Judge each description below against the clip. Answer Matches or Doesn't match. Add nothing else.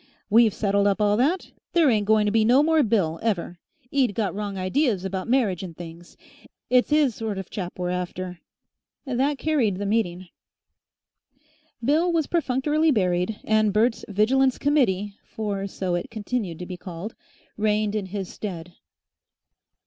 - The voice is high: Matches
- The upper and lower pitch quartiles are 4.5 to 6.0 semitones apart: Matches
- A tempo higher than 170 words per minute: Doesn't match